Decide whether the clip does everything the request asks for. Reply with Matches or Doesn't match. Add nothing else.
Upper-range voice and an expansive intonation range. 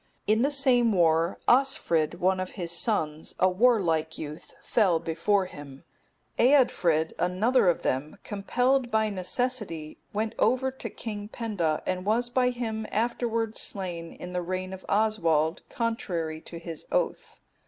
Matches